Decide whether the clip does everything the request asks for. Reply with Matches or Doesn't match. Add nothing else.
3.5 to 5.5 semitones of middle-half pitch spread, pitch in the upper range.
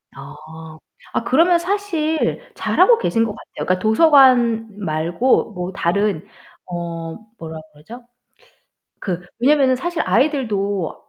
Doesn't match